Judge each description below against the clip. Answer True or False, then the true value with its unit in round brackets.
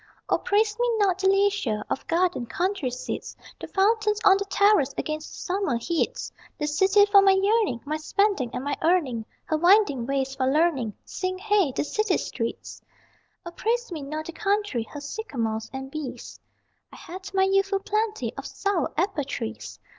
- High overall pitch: True (360 Hz)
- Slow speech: False (175 wpm)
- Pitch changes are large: True (6.7 semitones)